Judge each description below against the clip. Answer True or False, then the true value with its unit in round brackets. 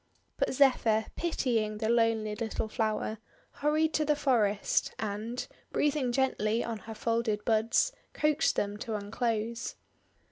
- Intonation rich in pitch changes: False (3.3 semitones)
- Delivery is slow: True (130 wpm)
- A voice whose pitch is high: True (230 Hz)